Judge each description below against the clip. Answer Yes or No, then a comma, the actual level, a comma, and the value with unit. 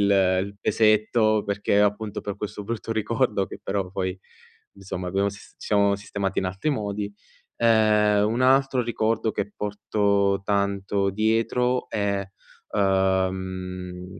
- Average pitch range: No, narrow, 1.9 semitones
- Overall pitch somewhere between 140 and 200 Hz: No, low, 100 Hz